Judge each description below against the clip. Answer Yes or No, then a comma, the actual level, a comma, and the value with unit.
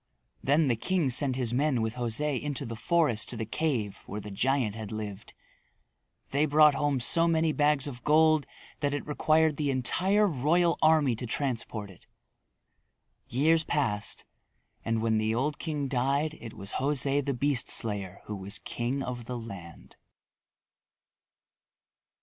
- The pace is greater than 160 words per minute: No, average, 155 wpm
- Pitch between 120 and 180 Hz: Yes, low, 135 Hz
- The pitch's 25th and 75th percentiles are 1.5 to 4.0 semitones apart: No, average, 4.8 semitones